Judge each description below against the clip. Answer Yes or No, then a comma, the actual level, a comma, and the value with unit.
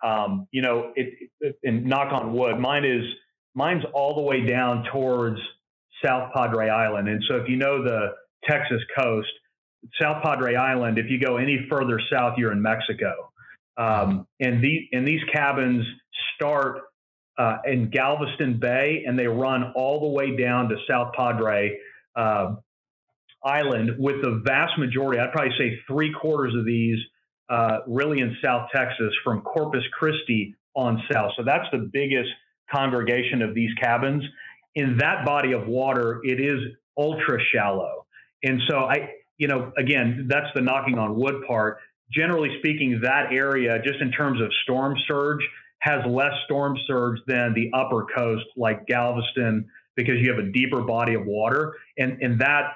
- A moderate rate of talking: Yes, average, 165 wpm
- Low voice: Yes, low, 125 Hz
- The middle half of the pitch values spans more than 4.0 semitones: No, average, 2.9 semitones